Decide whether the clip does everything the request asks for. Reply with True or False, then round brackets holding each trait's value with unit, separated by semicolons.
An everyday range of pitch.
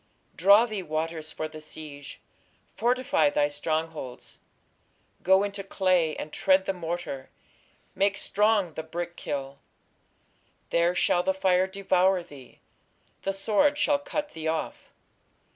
True (3.8 semitones)